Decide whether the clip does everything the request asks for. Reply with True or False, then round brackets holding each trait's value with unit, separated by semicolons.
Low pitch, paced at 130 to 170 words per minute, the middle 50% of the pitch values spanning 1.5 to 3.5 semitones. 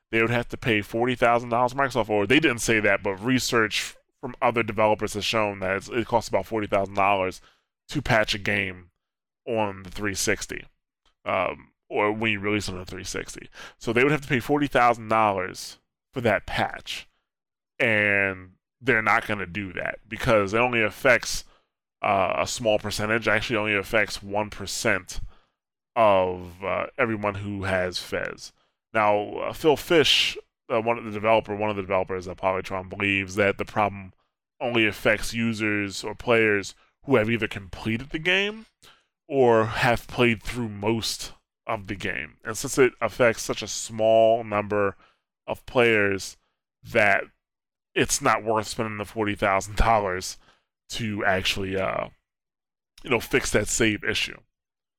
True (105 Hz; 155 wpm; 2.4 semitones)